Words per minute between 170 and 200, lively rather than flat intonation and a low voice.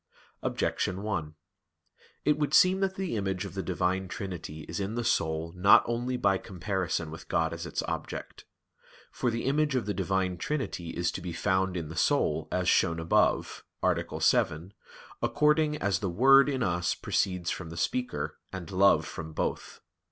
Yes: average, 175 wpm; wide, 6.2 semitones; very low, 95 Hz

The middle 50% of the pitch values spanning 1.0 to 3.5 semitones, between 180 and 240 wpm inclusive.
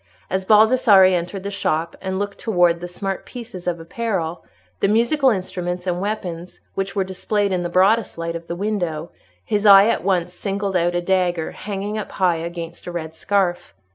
Yes: average, 2.7 semitones; average, 185 wpm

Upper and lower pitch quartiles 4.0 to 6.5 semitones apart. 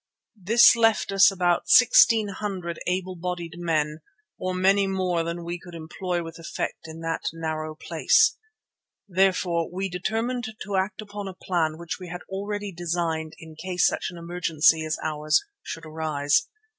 No: average, 2.9 semitones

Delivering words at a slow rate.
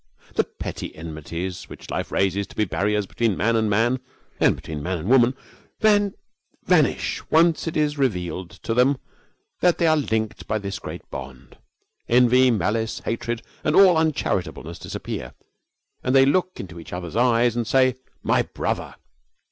No: average, 155 wpm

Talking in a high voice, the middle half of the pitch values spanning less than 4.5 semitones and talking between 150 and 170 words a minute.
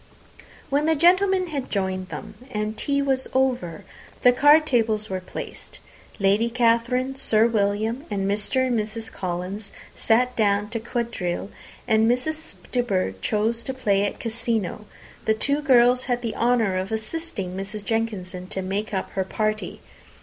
Yes: high, 225 Hz; average, 3.9 semitones; average, 155 wpm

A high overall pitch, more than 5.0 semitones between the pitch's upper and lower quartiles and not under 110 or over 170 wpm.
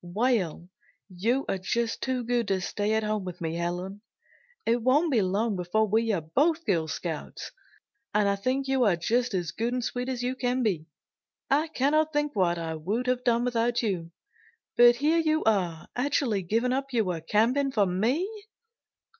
No: high, 225 Hz; wide, 5.4 semitones; average, 180 wpm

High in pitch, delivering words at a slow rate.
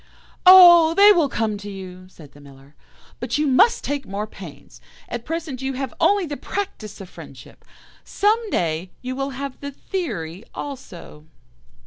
No: very high, 260 Hz; average, 160 wpm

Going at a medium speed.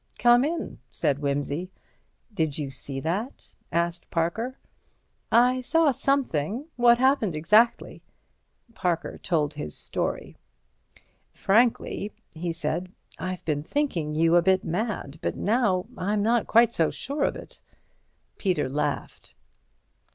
No: slow, 120 wpm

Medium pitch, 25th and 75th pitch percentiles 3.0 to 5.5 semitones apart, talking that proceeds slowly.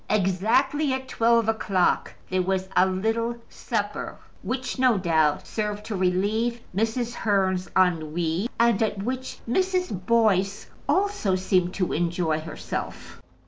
No: high, 205 Hz; average, 4.1 semitones; slow, 125 wpm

